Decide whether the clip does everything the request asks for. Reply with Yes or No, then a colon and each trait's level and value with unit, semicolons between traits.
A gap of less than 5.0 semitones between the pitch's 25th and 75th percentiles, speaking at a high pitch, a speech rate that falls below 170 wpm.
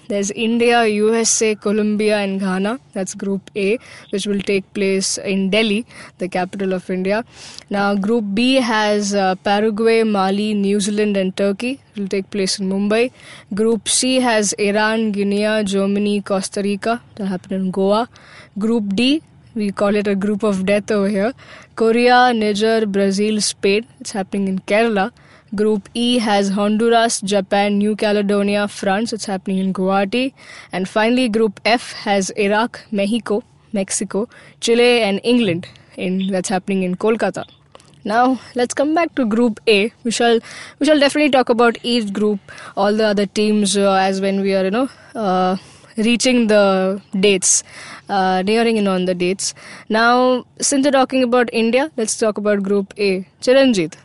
Yes: average, 2.7 semitones; high, 210 Hz; average, 160 wpm